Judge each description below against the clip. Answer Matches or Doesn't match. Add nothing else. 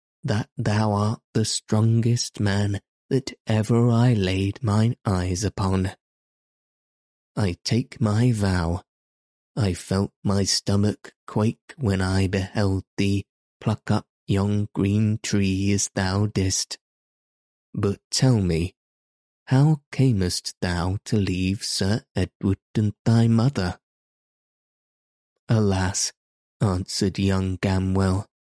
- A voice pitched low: Matches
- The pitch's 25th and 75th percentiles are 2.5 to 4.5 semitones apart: Matches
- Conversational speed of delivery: Doesn't match